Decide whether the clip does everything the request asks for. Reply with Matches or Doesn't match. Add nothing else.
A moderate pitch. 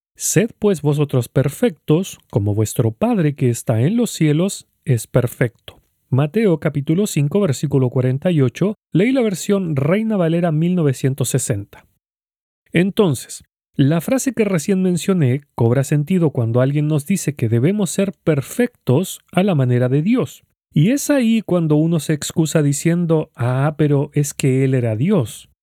Matches